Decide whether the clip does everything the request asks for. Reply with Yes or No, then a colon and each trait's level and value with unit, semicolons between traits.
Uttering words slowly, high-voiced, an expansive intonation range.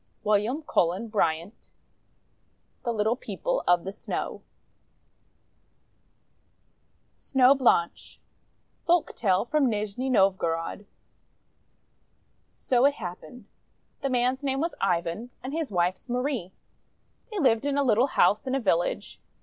Yes: slow, 115 wpm; high, 235 Hz; wide, 5.8 semitones